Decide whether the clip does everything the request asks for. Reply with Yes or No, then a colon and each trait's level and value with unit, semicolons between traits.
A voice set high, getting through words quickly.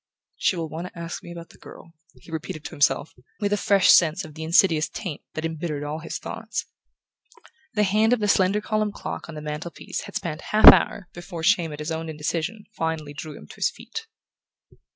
No: medium, 165 Hz; fast, 215 wpm